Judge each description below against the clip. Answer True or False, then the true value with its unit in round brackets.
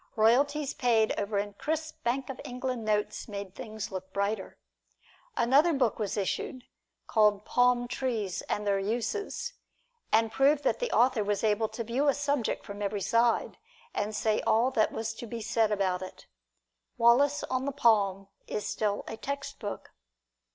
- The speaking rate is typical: True (160 wpm)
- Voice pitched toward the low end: False (225 Hz)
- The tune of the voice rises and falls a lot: False (3.9 semitones)